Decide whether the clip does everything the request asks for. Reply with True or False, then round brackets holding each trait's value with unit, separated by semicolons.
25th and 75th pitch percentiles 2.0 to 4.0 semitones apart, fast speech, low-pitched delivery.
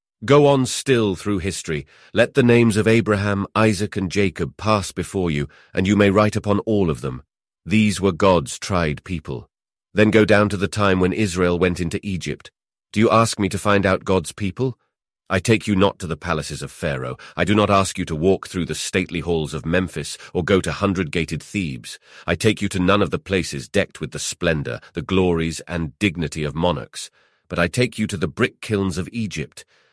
True (3.3 semitones; 210 wpm; 100 Hz)